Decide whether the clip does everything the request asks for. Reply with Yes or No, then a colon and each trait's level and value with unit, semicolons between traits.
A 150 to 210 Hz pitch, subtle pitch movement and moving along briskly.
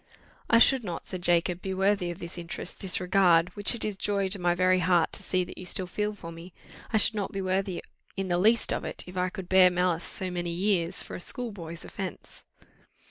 Yes: medium, 185 Hz; narrow, 2.1 semitones; fast, 230 wpm